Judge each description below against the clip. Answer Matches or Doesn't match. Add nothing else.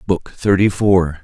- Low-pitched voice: Matches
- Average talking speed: Matches